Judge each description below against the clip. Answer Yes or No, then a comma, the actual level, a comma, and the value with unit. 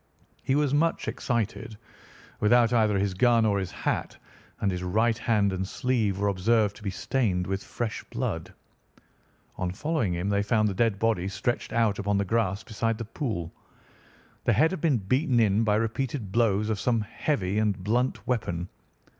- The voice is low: Yes, low, 110 Hz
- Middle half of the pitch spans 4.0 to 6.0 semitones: No, average, 3.2 semitones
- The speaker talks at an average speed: Yes, average, 175 wpm